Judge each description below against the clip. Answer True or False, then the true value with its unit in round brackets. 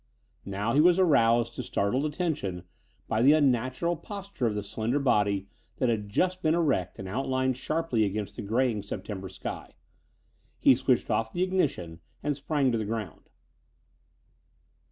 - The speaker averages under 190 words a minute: True (155 wpm)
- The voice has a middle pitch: False (120 Hz)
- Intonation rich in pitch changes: True (6.5 semitones)